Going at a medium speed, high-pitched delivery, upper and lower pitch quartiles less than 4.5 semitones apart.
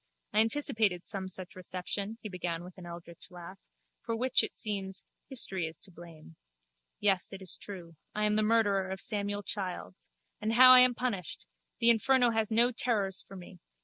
Yes: average, 180 wpm; high, 200 Hz; average, 3.7 semitones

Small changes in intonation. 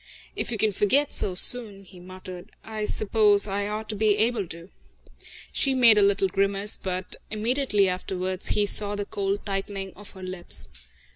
Yes: narrow, 2.0 semitones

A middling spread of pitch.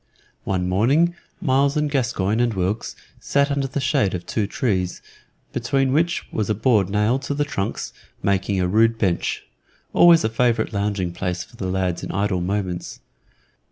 No: wide, 6.0 semitones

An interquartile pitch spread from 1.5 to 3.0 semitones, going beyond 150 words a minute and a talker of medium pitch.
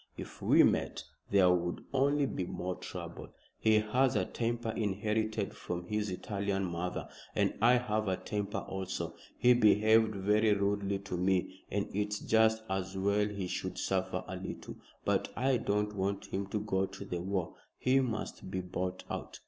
No: narrow, 2.5 semitones; average, 170 wpm; low, 100 Hz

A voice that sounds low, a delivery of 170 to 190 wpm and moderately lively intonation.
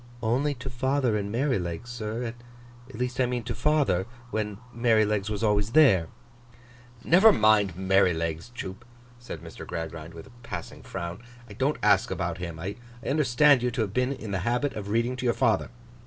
Yes: low, 110 Hz; average, 175 wpm; average, 4.5 semitones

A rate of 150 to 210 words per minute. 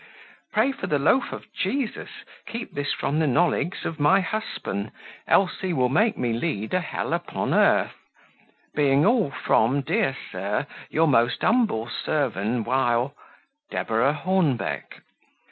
No: average, 140 wpm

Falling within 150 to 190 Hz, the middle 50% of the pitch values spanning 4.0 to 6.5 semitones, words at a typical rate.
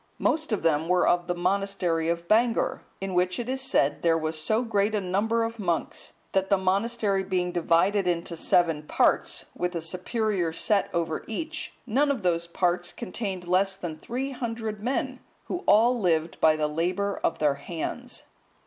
Yes: medium, 185 Hz; average, 4.7 semitones; average, 175 wpm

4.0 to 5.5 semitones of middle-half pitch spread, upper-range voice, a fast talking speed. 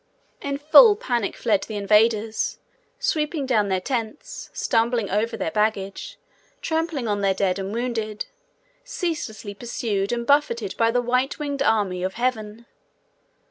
No: average, 4.7 semitones; high, 230 Hz; average, 140 wpm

